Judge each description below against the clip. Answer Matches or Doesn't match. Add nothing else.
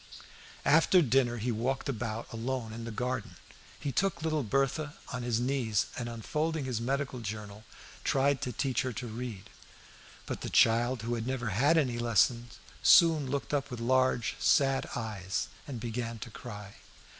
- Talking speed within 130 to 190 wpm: Matches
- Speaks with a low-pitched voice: Matches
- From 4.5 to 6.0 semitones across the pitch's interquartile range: Doesn't match